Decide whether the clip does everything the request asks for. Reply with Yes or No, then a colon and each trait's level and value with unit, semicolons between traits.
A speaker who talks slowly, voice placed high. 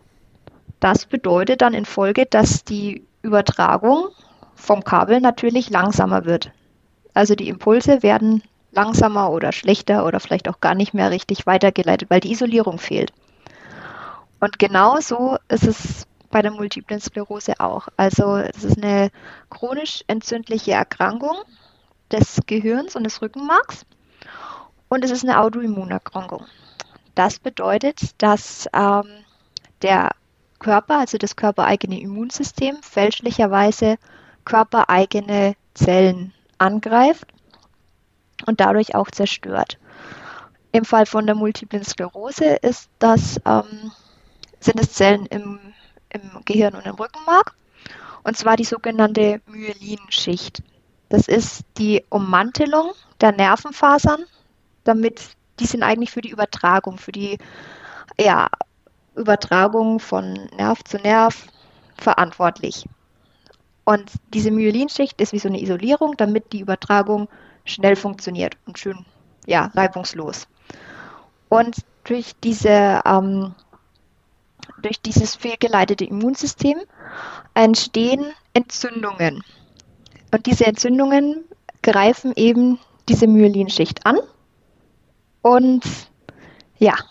Yes: slow, 110 wpm; high, 215 Hz